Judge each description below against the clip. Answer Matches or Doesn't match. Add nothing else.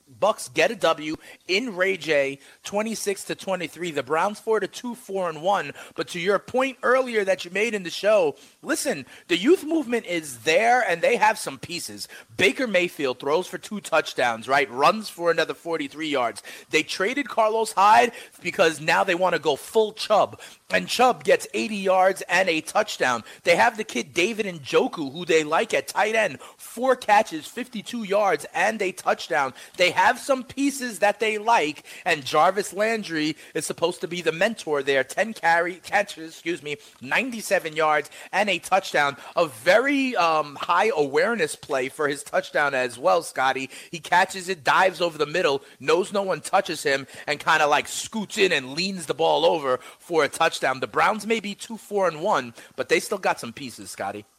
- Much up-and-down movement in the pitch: Matches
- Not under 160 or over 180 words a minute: Doesn't match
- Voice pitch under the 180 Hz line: Doesn't match